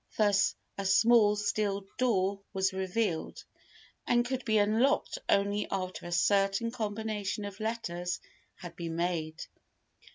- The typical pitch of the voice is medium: No, high, 200 Hz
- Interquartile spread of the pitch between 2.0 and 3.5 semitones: Yes, average, 2.8 semitones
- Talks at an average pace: No, slow, 125 wpm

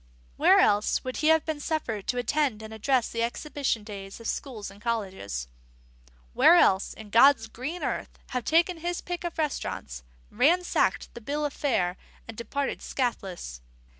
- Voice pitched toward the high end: Yes, high, 245 Hz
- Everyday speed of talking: Yes, average, 165 wpm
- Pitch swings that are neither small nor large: No, wide, 6.3 semitones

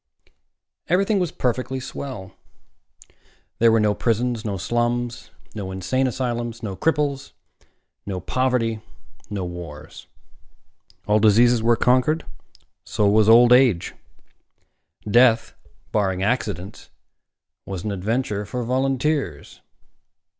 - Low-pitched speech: Yes, low, 115 Hz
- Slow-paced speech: Yes, slow, 105 wpm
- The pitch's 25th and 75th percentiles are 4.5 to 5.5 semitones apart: No, average, 3.8 semitones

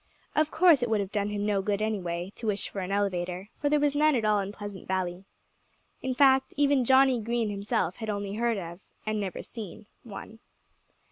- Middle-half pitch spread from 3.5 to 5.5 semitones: Yes, average, 4.0 semitones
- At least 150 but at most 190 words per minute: No, average, 200 wpm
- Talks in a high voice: Yes, high, 210 Hz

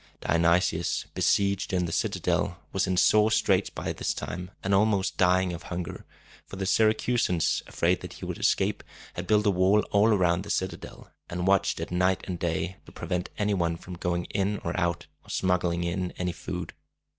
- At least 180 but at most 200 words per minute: Yes, average, 185 wpm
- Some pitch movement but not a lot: No, narrow, 2.2 semitones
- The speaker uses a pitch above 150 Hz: No, very low, 90 Hz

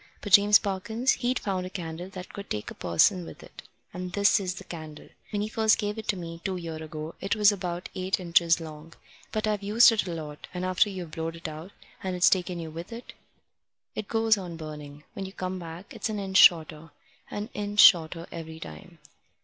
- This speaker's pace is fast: Yes, fast, 215 wpm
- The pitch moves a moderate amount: Yes, average, 3.7 semitones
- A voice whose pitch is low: No, medium, 180 Hz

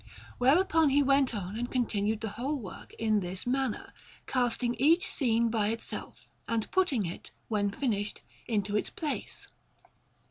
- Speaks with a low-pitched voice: No, high, 235 Hz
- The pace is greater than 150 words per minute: No, average, 145 wpm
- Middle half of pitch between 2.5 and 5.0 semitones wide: Yes, average, 4.5 semitones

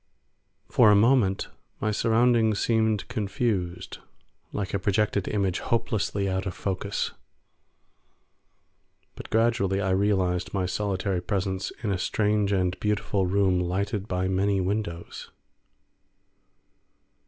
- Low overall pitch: Yes, low, 100 Hz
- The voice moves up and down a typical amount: No, narrow, 2.2 semitones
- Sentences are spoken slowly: Yes, slow, 110 wpm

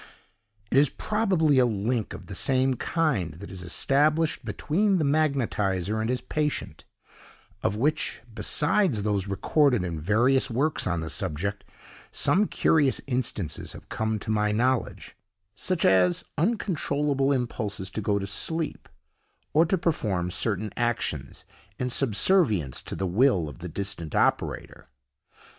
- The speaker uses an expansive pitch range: Yes, wide, 7.1 semitones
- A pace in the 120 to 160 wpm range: Yes, average, 140 wpm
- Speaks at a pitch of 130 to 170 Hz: No, low, 120 Hz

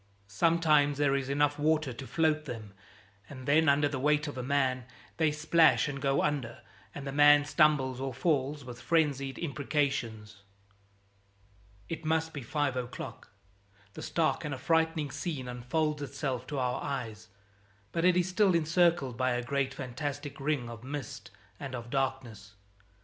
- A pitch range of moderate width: Yes, average, 3.0 semitones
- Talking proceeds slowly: No, average, 155 wpm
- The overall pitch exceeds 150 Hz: No, medium, 140 Hz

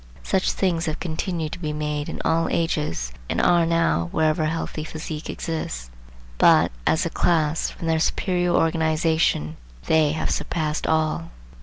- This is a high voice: No, medium, 160 Hz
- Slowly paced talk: No, average, 155 wpm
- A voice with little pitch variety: Yes, narrow, 1.5 semitones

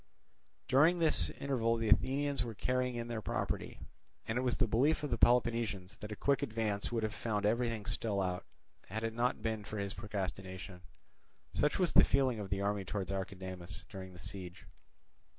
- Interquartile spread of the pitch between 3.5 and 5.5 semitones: Yes, average, 3.8 semitones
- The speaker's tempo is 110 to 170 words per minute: No, average, 185 wpm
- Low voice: Yes, low, 110 Hz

